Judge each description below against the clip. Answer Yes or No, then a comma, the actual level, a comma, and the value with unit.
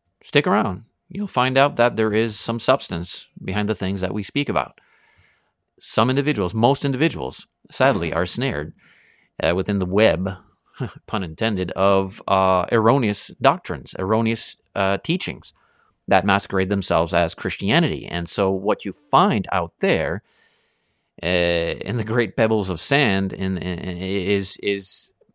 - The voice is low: Yes, low, 100 Hz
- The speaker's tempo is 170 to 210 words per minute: No, average, 140 wpm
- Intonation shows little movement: No, average, 3.2 semitones